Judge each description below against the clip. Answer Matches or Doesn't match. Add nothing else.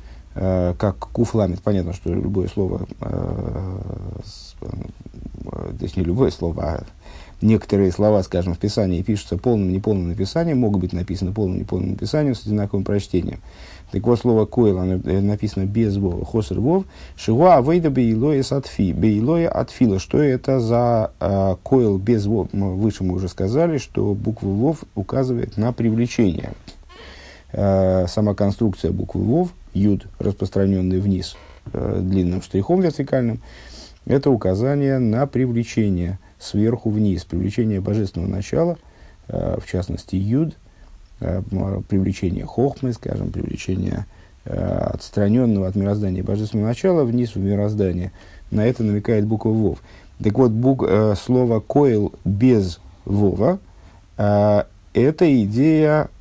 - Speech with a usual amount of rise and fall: Matches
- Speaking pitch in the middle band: Doesn't match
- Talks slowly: Doesn't match